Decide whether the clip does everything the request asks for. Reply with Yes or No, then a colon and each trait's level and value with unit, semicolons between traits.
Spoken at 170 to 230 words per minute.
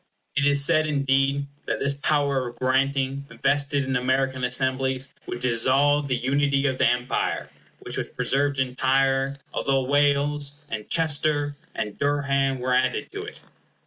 No: average, 145 wpm